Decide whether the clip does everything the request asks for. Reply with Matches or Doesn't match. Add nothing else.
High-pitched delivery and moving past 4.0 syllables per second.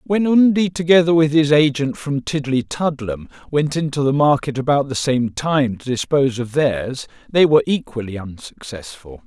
Doesn't match